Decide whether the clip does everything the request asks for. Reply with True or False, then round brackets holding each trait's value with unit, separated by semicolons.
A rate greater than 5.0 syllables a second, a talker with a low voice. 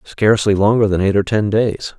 True (5.3 syllables/s; 105 Hz)